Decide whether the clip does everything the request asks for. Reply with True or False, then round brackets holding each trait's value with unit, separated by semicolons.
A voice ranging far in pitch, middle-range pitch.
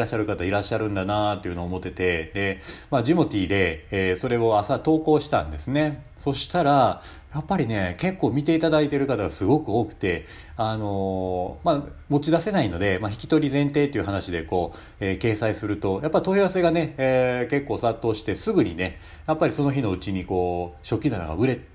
False (7.4 semitones; 110 Hz)